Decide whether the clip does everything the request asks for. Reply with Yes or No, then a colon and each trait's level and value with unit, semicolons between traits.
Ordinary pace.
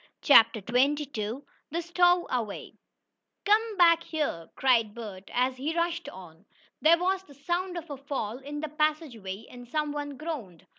Yes: average, 150 wpm